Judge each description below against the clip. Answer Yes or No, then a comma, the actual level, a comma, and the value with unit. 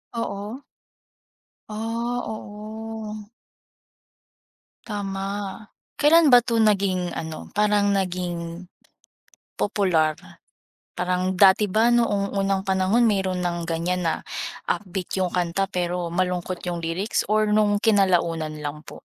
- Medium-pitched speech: No, high, 195 Hz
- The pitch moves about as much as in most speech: Yes, average, 3.0 semitones